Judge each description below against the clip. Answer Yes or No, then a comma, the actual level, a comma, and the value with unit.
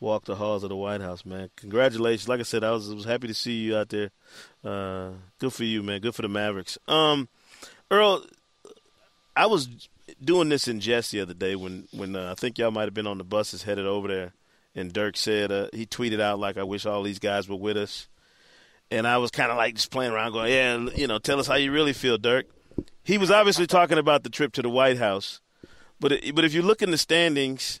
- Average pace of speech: No, fast, 240 wpm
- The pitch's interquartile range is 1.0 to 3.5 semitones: No, average, 4.6 semitones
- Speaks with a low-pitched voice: Yes, low, 110 Hz